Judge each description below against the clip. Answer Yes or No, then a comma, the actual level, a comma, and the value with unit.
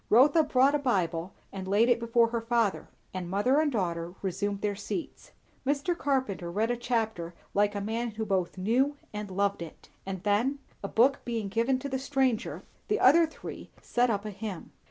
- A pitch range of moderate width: Yes, average, 4.8 semitones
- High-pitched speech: Yes, high, 225 Hz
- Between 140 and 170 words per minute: No, average, 190 wpm